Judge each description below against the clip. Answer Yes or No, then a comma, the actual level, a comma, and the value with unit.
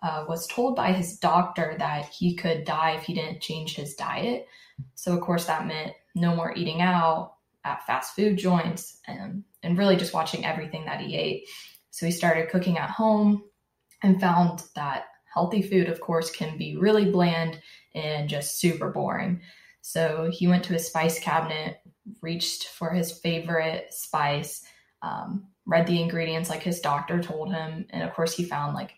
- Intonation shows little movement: Yes, narrow, 2.0 semitones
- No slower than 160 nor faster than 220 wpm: Yes, average, 180 wpm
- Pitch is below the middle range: No, medium, 170 Hz